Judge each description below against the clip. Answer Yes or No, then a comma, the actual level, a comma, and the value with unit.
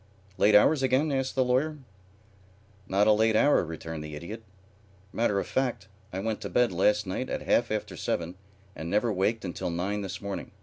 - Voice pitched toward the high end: No, low, 105 Hz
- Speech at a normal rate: Yes, average, 185 wpm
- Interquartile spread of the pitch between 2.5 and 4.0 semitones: No, average, 4.6 semitones